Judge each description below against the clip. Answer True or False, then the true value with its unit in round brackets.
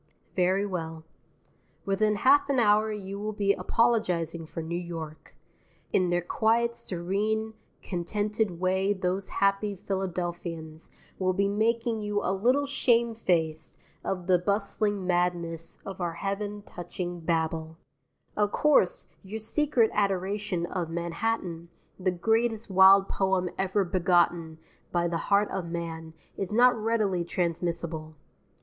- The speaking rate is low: True (130 wpm)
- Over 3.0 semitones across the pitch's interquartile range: True (3.6 semitones)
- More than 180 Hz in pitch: True (190 Hz)